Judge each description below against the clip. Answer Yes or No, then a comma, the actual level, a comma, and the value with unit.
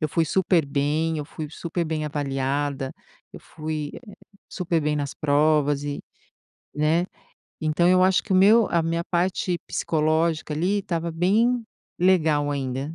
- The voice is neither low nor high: Yes, medium, 160 Hz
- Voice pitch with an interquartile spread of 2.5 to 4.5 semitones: Yes, average, 2.9 semitones